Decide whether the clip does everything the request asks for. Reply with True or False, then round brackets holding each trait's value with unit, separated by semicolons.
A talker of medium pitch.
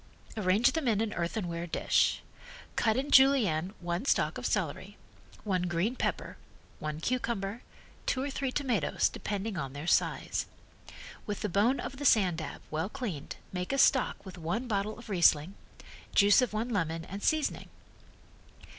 False (205 Hz)